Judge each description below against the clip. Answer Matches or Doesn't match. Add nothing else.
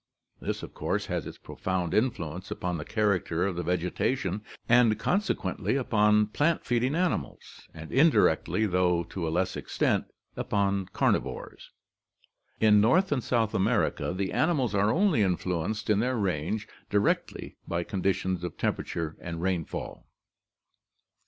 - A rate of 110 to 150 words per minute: Matches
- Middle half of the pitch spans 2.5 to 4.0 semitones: Doesn't match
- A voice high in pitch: Doesn't match